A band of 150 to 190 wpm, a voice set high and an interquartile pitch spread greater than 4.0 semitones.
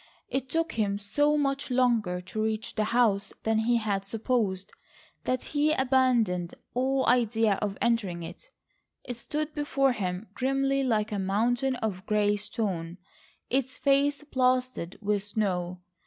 No: average, 140 wpm; high, 230 Hz; average, 4.5 semitones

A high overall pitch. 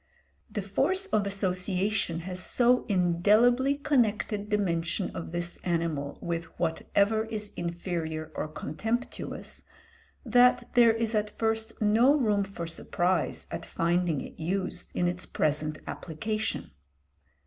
Yes: high, 195 Hz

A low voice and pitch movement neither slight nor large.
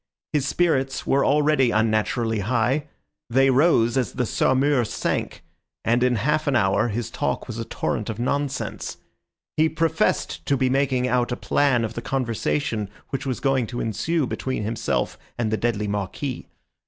Yes: low, 125 Hz; average, 3.5 semitones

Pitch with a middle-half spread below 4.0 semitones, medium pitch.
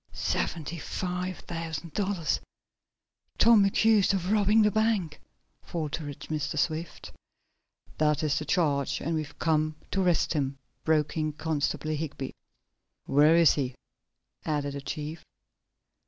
Yes: average, 3.3 semitones; medium, 160 Hz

